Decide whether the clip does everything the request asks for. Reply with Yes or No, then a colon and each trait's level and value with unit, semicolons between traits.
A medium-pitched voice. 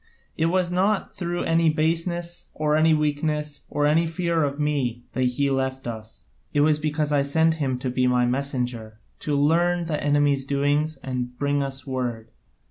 Yes: medium, 145 Hz